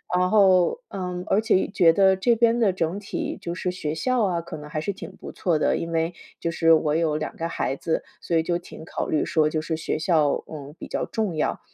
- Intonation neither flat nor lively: Yes, average, 3.3 semitones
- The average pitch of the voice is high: No, medium, 170 Hz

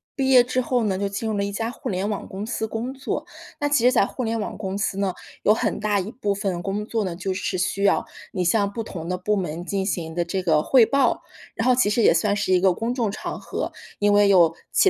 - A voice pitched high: Yes, high, 205 Hz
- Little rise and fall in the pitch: No, average, 3.2 semitones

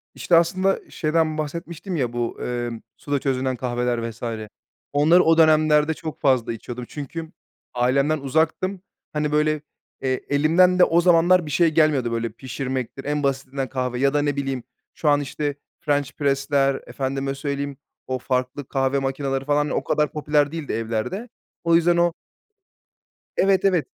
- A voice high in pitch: No, medium, 145 Hz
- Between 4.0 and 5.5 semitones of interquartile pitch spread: No, average, 3.3 semitones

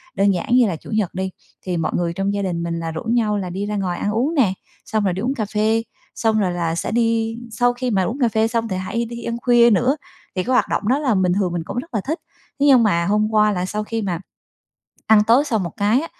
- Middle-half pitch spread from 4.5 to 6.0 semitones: No, average, 3.9 semitones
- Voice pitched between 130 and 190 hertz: No, high, 215 Hz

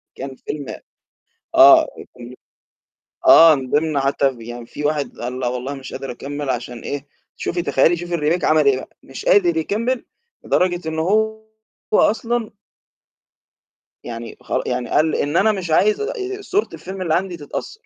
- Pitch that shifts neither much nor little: No, wide, 7.7 semitones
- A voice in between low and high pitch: Yes, medium, 160 Hz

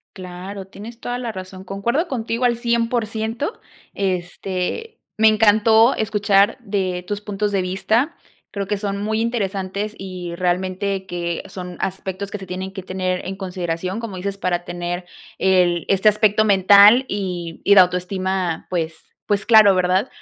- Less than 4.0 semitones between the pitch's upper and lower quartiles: Yes, average, 2.9 semitones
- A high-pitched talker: Yes, high, 195 Hz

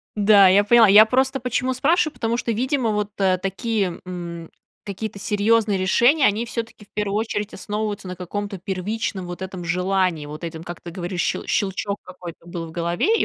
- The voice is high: Yes, high, 200 Hz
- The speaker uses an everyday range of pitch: Yes, average, 3.7 semitones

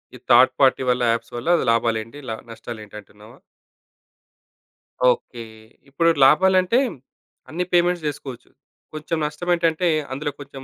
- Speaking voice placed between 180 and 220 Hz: No, medium, 140 Hz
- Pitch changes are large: Yes, wide, 6.2 semitones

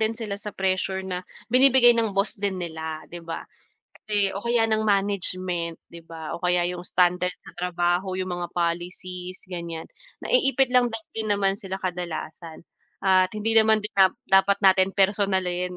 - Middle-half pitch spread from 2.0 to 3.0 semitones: Yes, average, 2.7 semitones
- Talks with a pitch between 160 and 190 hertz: Yes, medium, 185 Hz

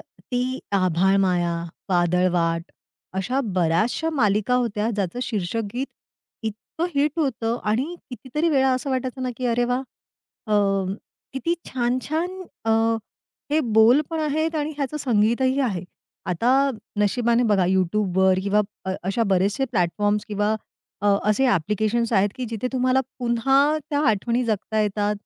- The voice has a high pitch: Yes, high, 230 Hz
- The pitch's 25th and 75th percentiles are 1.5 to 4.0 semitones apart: No, average, 4.8 semitones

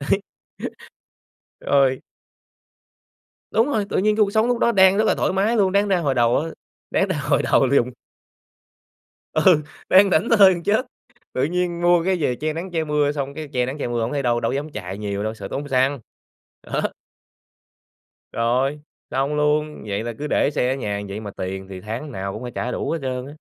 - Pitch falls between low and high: Yes, medium, 145 Hz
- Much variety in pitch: Yes, wide, 6.7 semitones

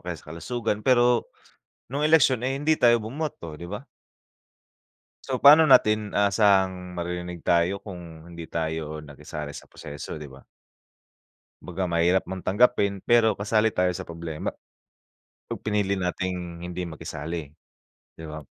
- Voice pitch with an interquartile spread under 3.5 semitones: No, average, 5.0 semitones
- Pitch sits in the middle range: No, very low, 90 Hz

